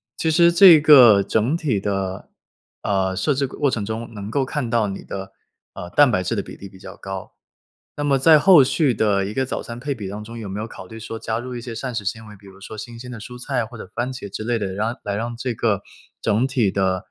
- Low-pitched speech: Yes, low, 115 Hz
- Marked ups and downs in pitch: No, average, 4.3 semitones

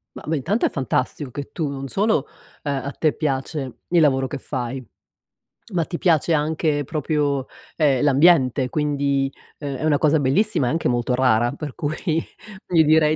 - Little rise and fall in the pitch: No, average, 3.0 semitones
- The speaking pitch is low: No, medium, 145 Hz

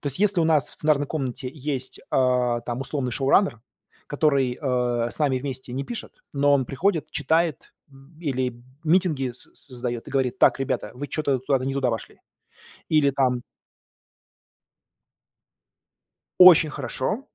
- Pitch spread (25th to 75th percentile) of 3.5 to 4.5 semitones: No, average, 3.1 semitones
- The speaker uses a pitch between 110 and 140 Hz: Yes, low, 135 Hz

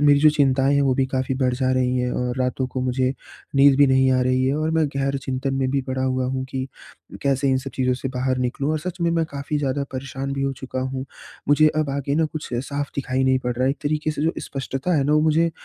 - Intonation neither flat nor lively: No, narrow, 1.7 semitones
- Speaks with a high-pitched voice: No, low, 135 Hz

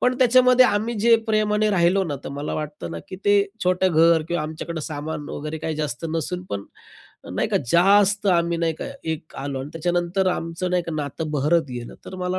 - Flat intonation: No, average, 3.9 semitones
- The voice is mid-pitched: Yes, medium, 170 Hz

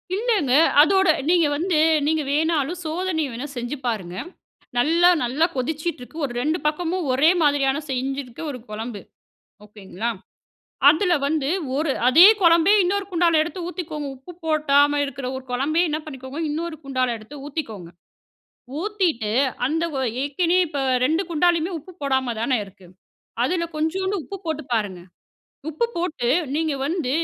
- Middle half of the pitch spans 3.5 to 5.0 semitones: Yes, average, 4.5 semitones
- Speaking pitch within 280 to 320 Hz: Yes, very high, 300 Hz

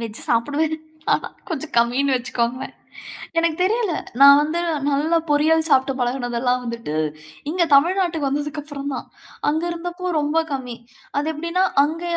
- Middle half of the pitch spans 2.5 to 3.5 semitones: No, average, 3.9 semitones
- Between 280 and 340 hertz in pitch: Yes, very high, 290 Hz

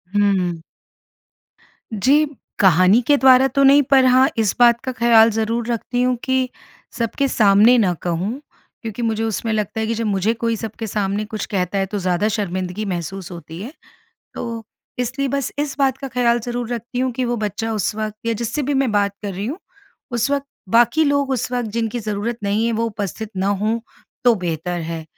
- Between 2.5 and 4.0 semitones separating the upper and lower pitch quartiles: Yes, average, 3.5 semitones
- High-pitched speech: Yes, high, 225 Hz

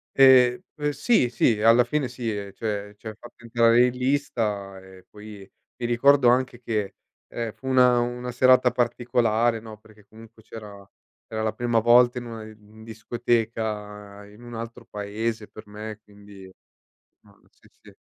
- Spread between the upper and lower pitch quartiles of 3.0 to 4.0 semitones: No, narrow, 2.5 semitones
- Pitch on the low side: Yes, low, 115 Hz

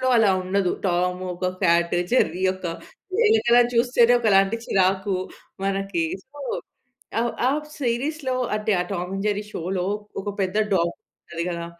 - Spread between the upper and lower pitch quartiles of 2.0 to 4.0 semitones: No, average, 4.4 semitones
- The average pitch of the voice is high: Yes, high, 195 Hz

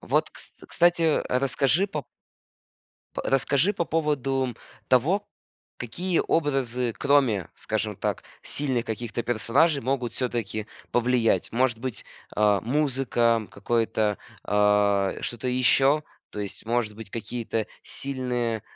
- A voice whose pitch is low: Yes, low, 125 Hz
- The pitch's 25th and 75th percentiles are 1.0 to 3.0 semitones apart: No, average, 3.6 semitones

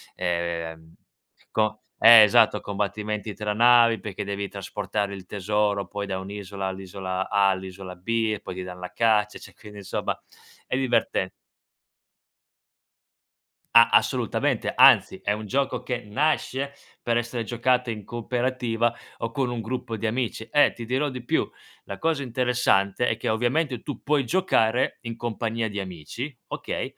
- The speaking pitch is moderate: No, low, 110 Hz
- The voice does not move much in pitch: No, average, 3.4 semitones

